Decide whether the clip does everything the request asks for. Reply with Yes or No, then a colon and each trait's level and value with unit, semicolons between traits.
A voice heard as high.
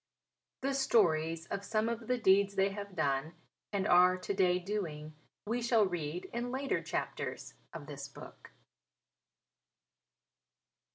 Yes: high, 195 Hz